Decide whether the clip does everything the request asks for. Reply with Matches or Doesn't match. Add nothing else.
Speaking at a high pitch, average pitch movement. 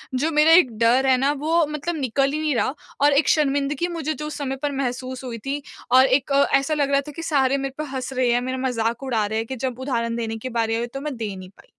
Matches